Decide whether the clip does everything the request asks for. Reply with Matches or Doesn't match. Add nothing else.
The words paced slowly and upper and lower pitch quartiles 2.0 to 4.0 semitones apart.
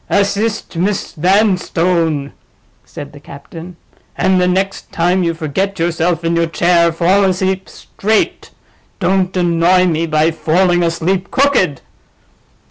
Matches